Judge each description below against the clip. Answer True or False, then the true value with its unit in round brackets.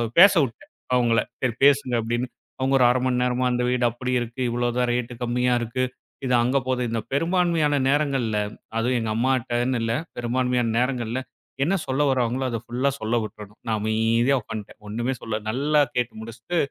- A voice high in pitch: False (125 Hz)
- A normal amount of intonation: False (2.1 semitones)